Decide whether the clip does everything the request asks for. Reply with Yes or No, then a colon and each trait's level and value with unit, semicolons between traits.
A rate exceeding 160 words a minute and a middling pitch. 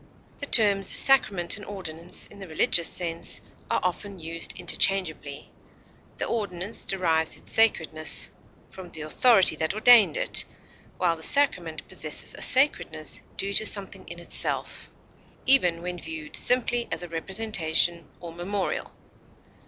No: slow, 135 wpm; medium, 180 Hz